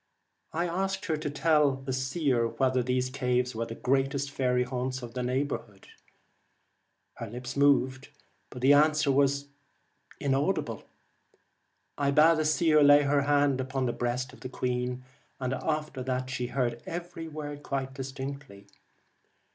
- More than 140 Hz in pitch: No, low, 135 Hz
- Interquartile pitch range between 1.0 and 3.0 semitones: Yes, narrow, 2.5 semitones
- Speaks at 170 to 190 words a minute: No, average, 145 wpm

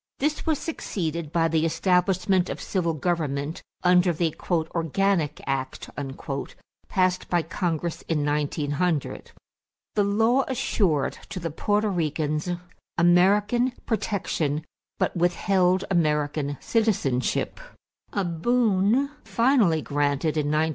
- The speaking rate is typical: No, slow, 105 wpm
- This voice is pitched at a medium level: Yes, medium, 175 Hz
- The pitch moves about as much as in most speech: Yes, average, 4.5 semitones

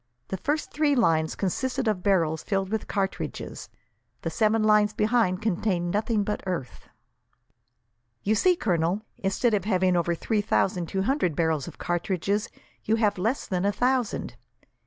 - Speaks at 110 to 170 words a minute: Yes, average, 155 wpm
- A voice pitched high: Yes, high, 200 Hz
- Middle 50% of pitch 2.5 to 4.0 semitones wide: Yes, average, 3.7 semitones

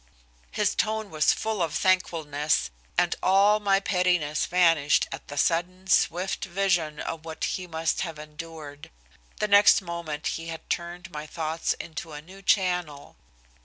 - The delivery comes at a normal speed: Yes, average, 150 wpm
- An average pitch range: Yes, average, 3.3 semitones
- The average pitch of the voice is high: No, medium, 170 Hz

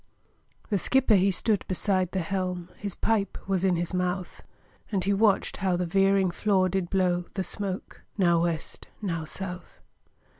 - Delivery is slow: No, average, 160 wpm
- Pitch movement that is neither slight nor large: No, narrow, 1.8 semitones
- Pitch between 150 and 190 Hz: Yes, medium, 185 Hz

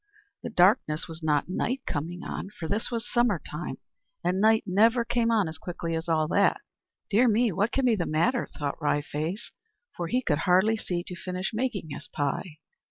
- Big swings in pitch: Yes, wide, 5.7 semitones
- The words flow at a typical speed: Yes, average, 195 wpm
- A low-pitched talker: No, medium, 185 Hz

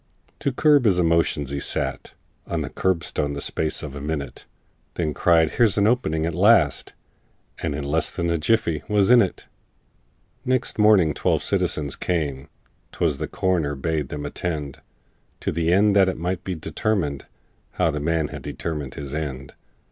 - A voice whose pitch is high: No, very low, 80 Hz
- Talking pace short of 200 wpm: Yes, average, 170 wpm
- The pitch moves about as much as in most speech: Yes, average, 4.4 semitones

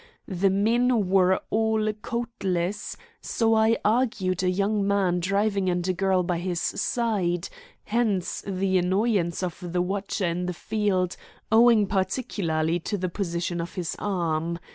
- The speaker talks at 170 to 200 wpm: No, average, 140 wpm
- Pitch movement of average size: Yes, average, 3.2 semitones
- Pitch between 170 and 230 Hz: Yes, high, 190 Hz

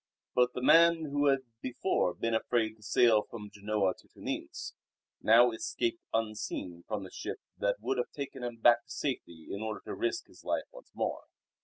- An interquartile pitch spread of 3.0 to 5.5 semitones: Yes, average, 5.2 semitones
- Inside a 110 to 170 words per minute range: No, average, 185 wpm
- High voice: No, low, 120 Hz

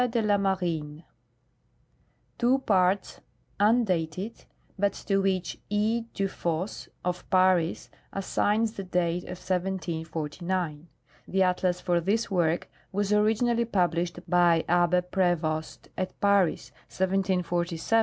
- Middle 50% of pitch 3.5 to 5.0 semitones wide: No, narrow, 2.6 semitones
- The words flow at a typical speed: No, slow, 115 wpm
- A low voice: No, medium, 185 Hz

